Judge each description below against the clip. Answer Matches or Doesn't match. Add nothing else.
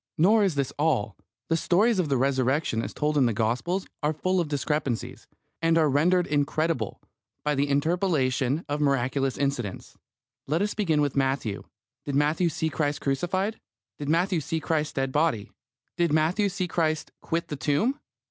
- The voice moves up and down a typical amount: Matches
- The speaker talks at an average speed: Matches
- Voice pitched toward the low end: Doesn't match